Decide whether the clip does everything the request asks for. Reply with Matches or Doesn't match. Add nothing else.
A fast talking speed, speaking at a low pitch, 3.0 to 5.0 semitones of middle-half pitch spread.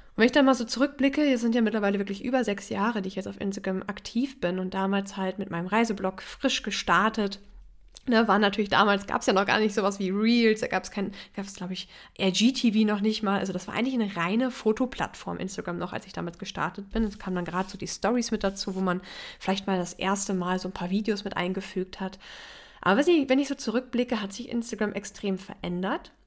Doesn't match